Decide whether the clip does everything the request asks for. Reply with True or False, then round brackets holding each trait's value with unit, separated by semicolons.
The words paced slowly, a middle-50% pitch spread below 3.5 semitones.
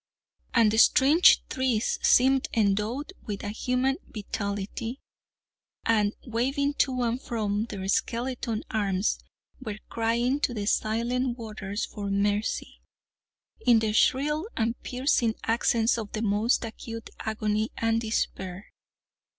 True (120 wpm; 2.9 semitones)